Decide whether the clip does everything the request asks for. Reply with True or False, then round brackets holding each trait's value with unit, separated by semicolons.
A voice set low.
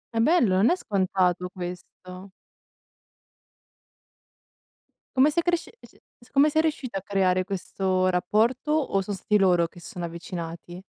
False (195 Hz)